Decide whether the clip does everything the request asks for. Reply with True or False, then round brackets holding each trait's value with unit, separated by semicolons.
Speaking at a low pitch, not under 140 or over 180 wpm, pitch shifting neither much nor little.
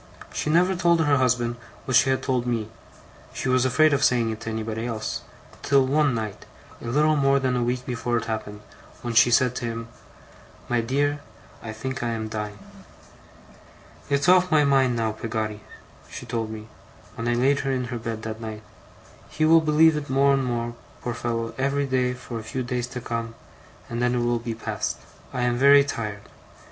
False (125 Hz; 200 wpm; 3.0 semitones)